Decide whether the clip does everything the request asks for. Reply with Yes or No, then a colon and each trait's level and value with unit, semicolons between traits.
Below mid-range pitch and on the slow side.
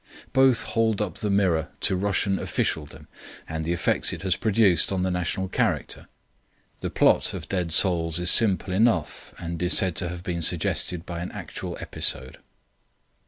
No: very low, 90 Hz; average, 165 wpm